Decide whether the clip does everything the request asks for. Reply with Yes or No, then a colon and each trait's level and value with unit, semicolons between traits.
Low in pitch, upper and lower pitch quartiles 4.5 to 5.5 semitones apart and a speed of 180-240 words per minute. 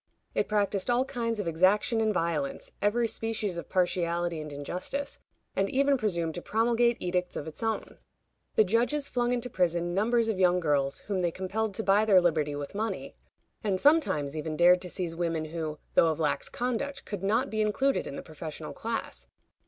No: high, 190 Hz; average, 5.2 semitones; average, 185 wpm